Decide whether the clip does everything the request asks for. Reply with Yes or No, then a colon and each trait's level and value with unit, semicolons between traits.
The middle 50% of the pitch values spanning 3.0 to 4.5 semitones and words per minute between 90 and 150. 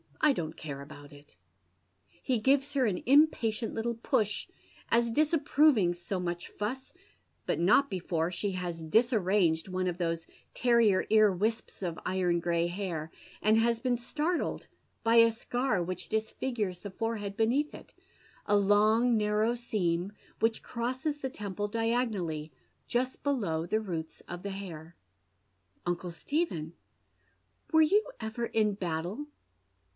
No: average, 5.3 semitones; average, 140 wpm